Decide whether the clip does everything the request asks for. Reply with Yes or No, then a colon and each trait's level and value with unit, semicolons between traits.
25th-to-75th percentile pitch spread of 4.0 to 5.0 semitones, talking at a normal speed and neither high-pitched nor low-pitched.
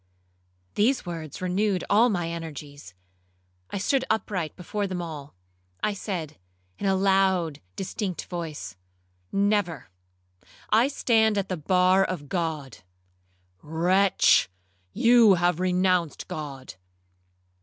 No: average, 4.3 semitones; slow, 105 wpm; medium, 180 Hz